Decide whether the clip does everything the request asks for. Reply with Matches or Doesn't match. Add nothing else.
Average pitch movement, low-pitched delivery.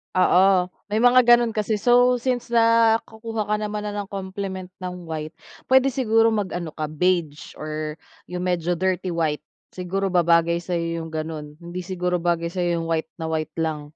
Doesn't match